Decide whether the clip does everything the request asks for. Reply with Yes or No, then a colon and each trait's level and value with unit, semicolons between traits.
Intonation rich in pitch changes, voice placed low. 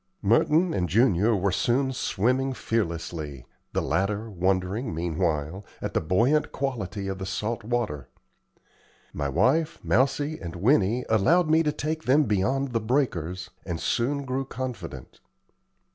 Yes: wide, 6.5 semitones; low, 110 Hz